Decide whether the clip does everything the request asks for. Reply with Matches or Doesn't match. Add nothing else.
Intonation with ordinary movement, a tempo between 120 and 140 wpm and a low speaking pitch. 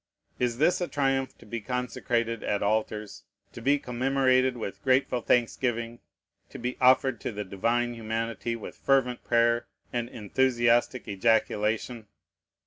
Doesn't match